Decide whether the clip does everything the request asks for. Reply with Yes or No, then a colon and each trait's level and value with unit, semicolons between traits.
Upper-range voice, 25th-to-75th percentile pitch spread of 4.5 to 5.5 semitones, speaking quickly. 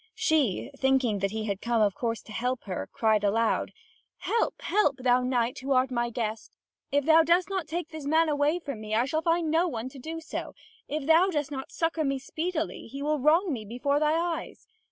Yes: very high, 275 Hz; average, 5.2 semitones; fast, 215 wpm